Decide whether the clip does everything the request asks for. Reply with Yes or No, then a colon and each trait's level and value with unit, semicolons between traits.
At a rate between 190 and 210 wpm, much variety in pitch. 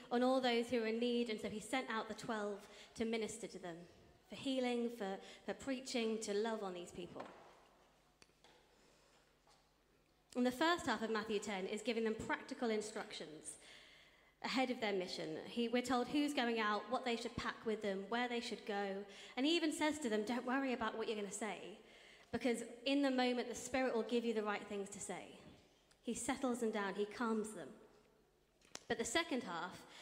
No: average, 200 wpm; average, 2.9 semitones